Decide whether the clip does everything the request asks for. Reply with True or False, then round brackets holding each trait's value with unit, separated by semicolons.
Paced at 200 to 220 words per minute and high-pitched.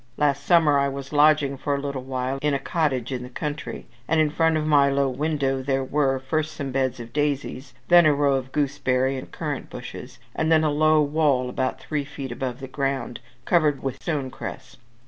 False (205 wpm; 140 Hz)